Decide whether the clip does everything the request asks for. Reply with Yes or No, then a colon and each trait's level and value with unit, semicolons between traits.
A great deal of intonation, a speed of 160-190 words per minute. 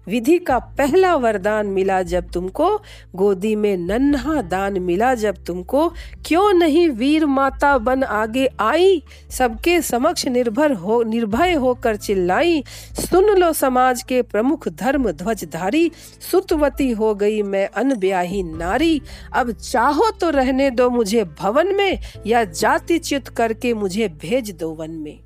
No: wide, 6.8 semitones; average, 140 wpm